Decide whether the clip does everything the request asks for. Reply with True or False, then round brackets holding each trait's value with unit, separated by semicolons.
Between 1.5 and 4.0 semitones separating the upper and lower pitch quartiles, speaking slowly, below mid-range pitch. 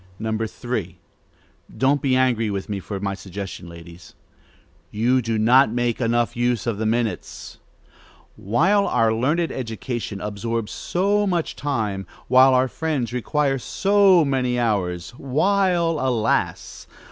False (4.6 semitones; 125 wpm; 120 Hz)